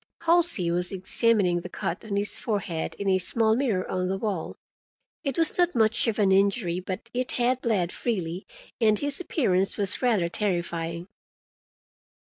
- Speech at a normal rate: Yes, average, 160 wpm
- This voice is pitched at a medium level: No, high, 200 Hz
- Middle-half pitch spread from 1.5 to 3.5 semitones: No, average, 4.5 semitones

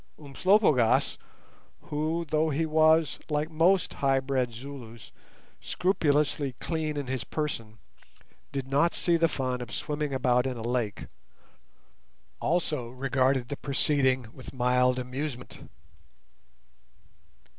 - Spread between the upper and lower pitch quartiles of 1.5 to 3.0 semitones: No, average, 3.5 semitones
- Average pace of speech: No, slow, 115 wpm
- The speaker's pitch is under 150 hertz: Yes, low, 135 Hz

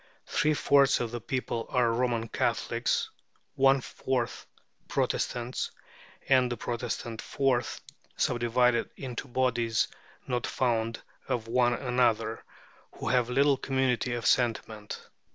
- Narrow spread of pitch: Yes, narrow, 1.8 semitones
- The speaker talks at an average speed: No, slow, 115 wpm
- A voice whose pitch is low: Yes, low, 125 Hz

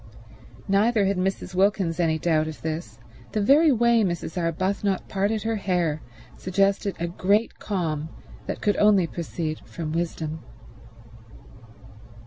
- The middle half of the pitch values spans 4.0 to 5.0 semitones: No, average, 3.6 semitones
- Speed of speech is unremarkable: No, slow, 125 wpm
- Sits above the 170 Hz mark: Yes, medium, 185 Hz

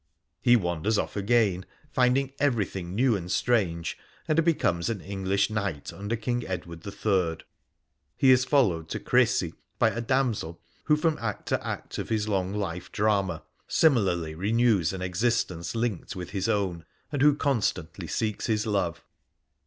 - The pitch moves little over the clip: No, average, 5.0 semitones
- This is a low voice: Yes, low, 100 Hz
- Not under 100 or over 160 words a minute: Yes, average, 155 wpm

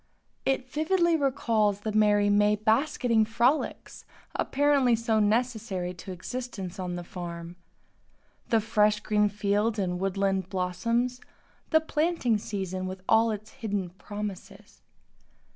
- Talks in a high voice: Yes, high, 210 Hz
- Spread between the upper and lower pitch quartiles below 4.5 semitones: Yes, average, 3.9 semitones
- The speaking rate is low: Yes, slow, 120 wpm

